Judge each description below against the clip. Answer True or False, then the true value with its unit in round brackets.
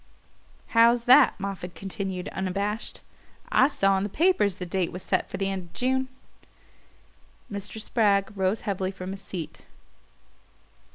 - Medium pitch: False (195 Hz)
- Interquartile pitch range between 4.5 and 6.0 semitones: False (3.0 semitones)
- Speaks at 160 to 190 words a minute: False (145 wpm)